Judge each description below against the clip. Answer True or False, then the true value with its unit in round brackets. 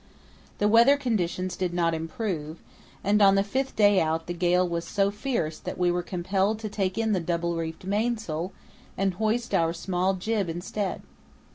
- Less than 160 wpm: False (175 wpm)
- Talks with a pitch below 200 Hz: True (185 Hz)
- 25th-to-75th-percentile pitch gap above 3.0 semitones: True (3.5 semitones)